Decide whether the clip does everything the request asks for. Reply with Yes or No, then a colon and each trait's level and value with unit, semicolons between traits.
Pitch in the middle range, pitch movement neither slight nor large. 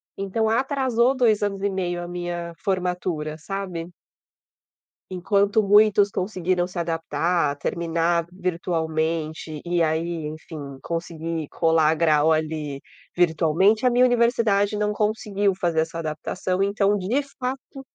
Yes: medium, 175 Hz; average, 3.9 semitones